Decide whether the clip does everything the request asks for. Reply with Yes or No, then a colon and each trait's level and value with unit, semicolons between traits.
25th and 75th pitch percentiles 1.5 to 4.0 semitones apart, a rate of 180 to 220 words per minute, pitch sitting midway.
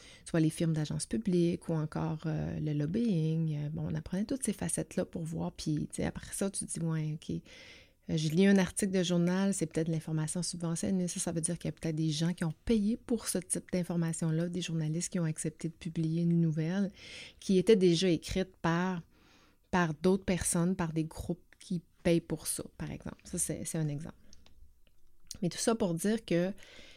Yes: narrow, 2.6 semitones; average, 205 wpm; medium, 170 Hz